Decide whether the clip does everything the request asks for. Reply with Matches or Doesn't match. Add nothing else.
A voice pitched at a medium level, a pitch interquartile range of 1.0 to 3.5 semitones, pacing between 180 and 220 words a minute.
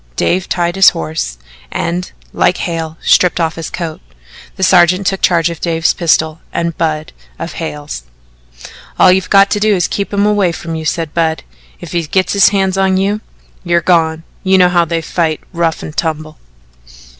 Matches